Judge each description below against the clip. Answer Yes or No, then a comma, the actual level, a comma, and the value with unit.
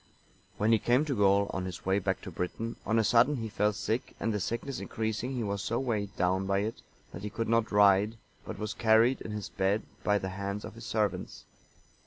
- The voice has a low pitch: Yes, low, 105 Hz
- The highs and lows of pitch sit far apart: No, narrow, 2.6 semitones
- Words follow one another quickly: Yes, fast, 225 wpm